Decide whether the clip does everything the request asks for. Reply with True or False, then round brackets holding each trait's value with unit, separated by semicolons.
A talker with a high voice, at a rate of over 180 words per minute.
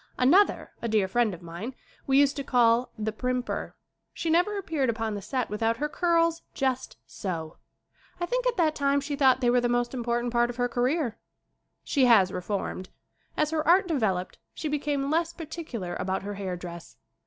True (250 Hz; 190 wpm)